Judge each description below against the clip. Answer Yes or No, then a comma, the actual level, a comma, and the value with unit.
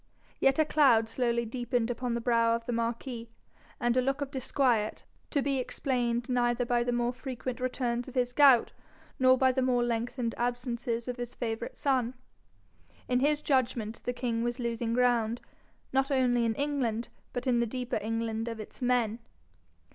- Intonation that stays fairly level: Yes, narrow, 1.7 semitones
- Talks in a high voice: Yes, high, 245 Hz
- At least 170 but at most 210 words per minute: Yes, average, 175 wpm